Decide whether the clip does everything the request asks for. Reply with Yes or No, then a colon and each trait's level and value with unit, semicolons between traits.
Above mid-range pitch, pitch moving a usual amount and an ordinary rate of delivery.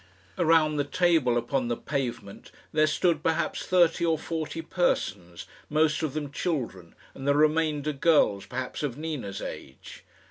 No: medium, 150 Hz; average, 4.3 semitones; average, 145 wpm